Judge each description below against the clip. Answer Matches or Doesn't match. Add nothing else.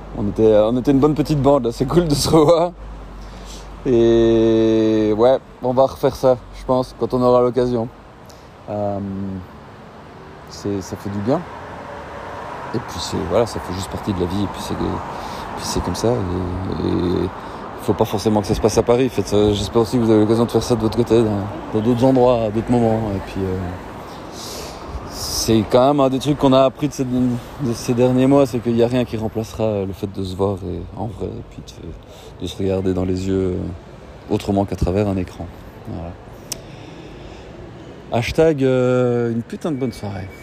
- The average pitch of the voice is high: Doesn't match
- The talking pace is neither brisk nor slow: Matches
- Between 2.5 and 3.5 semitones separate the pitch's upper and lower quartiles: Doesn't match